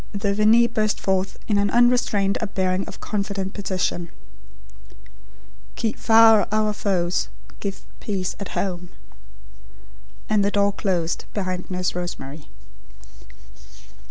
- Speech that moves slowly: Yes, slow, 115 wpm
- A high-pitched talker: Yes, high, 200 Hz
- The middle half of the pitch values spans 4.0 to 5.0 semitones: No, narrow, 2.5 semitones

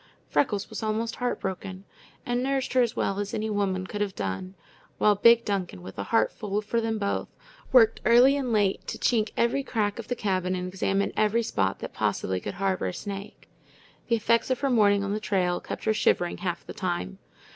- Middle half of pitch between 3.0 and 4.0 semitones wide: Yes, average, 3.5 semitones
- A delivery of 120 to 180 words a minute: No, fast, 205 wpm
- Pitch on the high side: Yes, high, 205 Hz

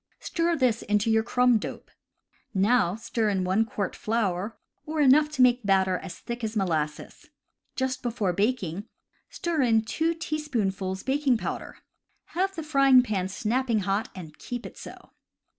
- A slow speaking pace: No, average, 160 wpm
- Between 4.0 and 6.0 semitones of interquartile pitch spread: Yes, average, 5.1 semitones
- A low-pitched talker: No, high, 225 Hz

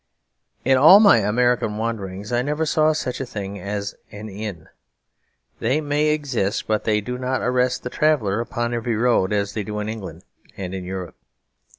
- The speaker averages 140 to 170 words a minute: No, average, 180 wpm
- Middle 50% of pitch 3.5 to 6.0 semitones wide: Yes, average, 3.9 semitones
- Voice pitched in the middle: No, low, 115 Hz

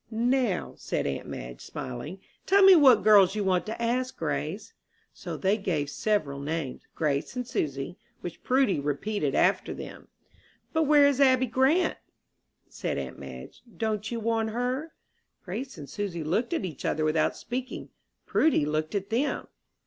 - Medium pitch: No, high, 210 Hz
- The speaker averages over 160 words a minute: No, average, 155 wpm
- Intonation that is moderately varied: No, wide, 8.4 semitones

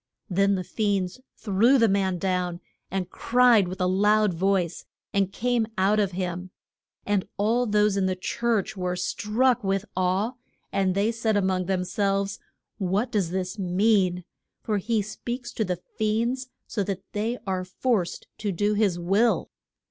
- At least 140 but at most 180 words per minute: Yes, average, 165 wpm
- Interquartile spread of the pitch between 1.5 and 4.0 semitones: Yes, average, 2.8 semitones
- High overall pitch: Yes, high, 200 Hz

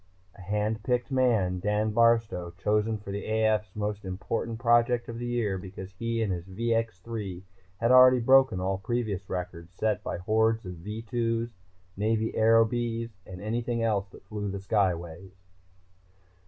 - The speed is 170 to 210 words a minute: No, average, 155 wpm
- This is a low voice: Yes, low, 110 Hz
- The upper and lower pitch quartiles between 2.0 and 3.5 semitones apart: Yes, average, 3.2 semitones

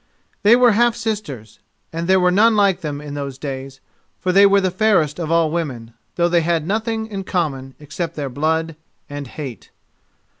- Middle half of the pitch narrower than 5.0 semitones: No, wide, 5.6 semitones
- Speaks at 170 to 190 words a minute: Yes, average, 185 wpm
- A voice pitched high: No, medium, 170 Hz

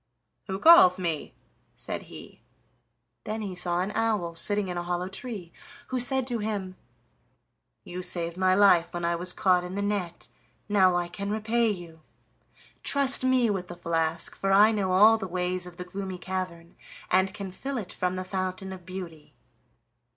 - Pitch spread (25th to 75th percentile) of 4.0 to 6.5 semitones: No, average, 2.7 semitones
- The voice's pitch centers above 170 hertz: Yes, medium, 185 Hz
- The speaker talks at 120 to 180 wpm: Yes, average, 175 wpm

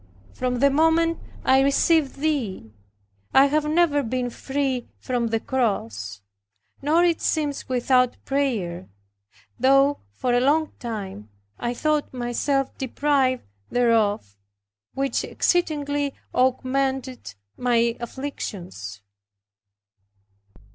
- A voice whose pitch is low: No, very high, 260 Hz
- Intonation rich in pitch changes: No, average, 3.4 semitones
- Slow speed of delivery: Yes, slow, 100 wpm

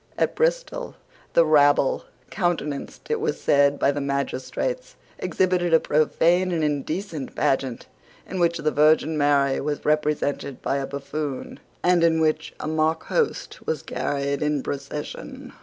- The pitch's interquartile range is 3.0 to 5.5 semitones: Yes, average, 3.5 semitones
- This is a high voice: No, medium, 155 Hz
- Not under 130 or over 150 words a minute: Yes, average, 140 wpm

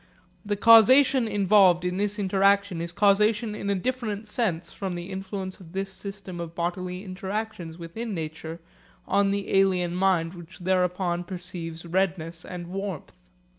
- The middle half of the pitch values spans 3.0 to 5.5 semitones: No, narrow, 2.5 semitones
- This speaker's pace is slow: No, average, 145 wpm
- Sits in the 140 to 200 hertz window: Yes, high, 190 Hz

